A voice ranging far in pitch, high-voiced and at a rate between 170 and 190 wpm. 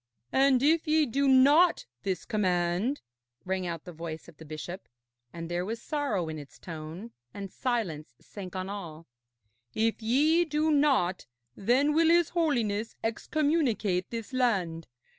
No: wide, 8.1 semitones; high, 220 Hz; average, 145 wpm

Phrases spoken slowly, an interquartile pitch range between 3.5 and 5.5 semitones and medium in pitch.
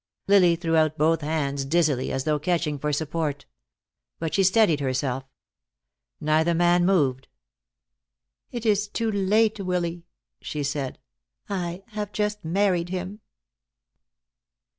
Yes: slow, 120 wpm; average, 4.4 semitones; medium, 170 Hz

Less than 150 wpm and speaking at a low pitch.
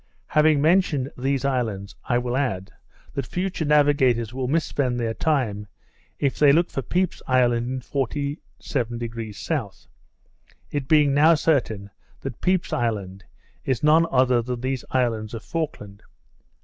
Yes: average, 140 wpm; low, 130 Hz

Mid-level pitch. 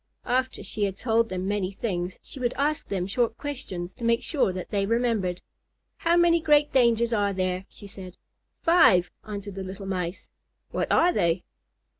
No: high, 205 Hz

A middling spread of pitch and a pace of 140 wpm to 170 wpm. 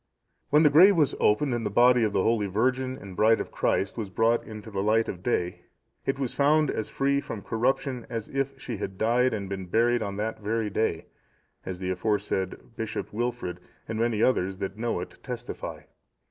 No: average, 3.8 semitones; average, 200 wpm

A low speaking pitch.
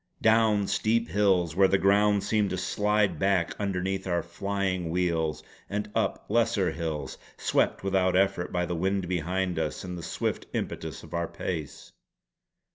Yes: very low, 95 Hz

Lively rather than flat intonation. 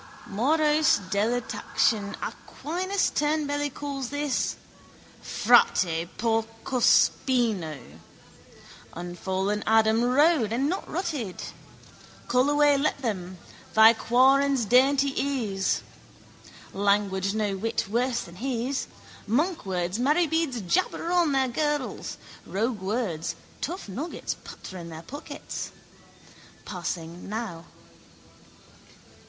Yes: wide, 6.4 semitones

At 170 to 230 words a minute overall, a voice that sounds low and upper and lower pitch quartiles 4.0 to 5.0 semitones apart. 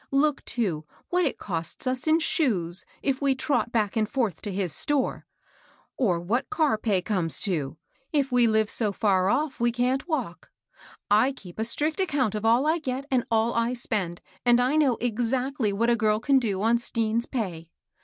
No: average, 190 wpm; high, 235 Hz; average, 4.6 semitones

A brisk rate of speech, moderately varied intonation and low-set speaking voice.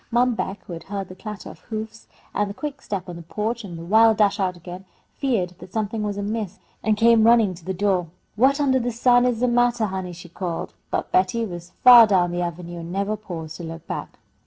No: fast, 230 wpm; average, 4.3 semitones; high, 205 Hz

